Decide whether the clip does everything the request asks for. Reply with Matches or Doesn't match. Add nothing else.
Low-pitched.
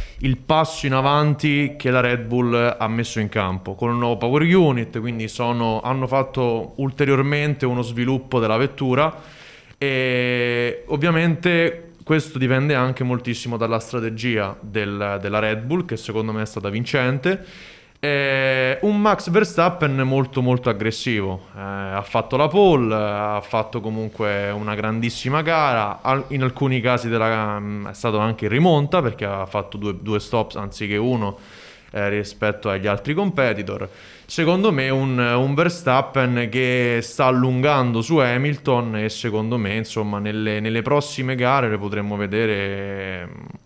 Matches